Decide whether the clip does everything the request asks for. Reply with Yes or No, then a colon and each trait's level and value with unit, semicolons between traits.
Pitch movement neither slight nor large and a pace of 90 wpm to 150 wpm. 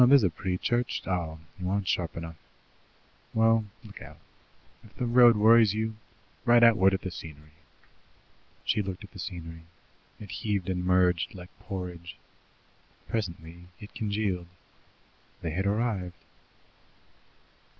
Yes: average, 3.9 semitones; slow, 135 wpm